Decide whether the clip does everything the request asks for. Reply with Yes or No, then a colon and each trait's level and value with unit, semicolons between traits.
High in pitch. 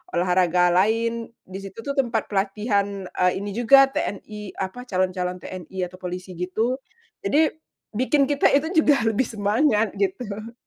Yes: high, 205 Hz